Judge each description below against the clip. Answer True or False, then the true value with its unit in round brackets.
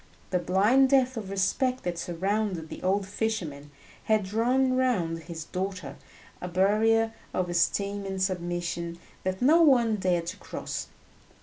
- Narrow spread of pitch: False (4.3 semitones)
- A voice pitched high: True (195 Hz)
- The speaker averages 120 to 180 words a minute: True (140 wpm)